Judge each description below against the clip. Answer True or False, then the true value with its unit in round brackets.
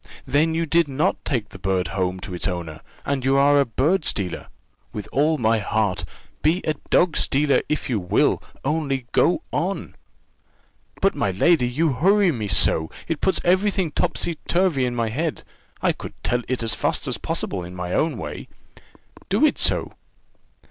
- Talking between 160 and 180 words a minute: True (175 wpm)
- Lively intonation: True (7.8 semitones)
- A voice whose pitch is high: False (135 Hz)